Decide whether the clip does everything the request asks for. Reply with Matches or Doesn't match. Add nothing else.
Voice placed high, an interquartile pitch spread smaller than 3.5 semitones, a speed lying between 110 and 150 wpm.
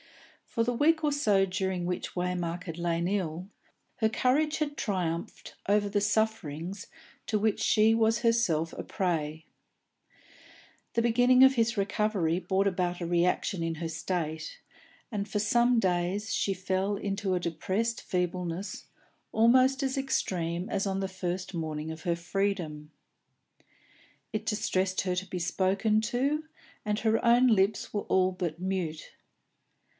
Doesn't match